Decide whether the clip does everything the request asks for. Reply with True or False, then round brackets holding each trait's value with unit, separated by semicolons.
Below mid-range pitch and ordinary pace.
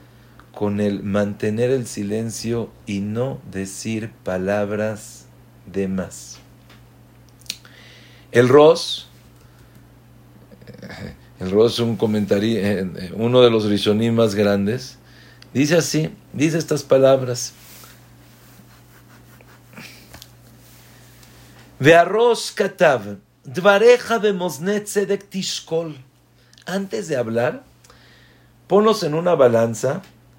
False (120 Hz; 80 wpm)